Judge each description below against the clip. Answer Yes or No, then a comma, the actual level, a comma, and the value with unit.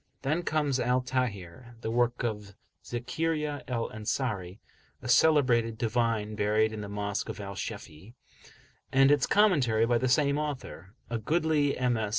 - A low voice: Yes, low, 120 Hz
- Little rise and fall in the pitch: No, average, 4.5 semitones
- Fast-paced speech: No, average, 150 wpm